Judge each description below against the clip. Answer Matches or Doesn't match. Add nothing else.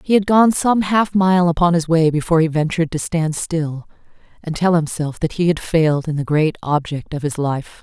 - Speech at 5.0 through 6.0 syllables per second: Matches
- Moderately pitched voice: Matches